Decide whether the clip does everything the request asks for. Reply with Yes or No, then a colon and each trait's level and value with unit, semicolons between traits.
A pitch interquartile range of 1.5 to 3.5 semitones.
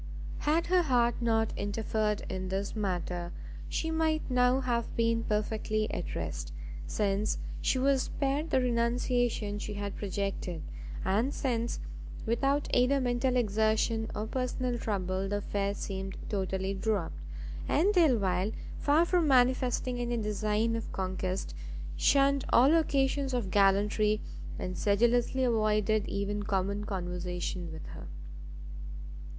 No: average, 4.1 semitones